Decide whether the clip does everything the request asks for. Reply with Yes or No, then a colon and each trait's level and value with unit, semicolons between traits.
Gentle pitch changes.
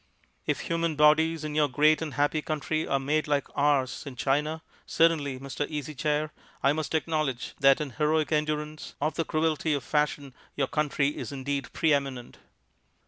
Yes: narrow, 1.8 semitones